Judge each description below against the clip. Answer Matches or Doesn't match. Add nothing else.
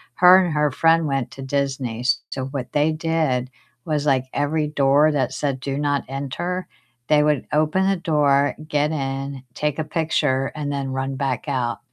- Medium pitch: Matches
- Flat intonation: Matches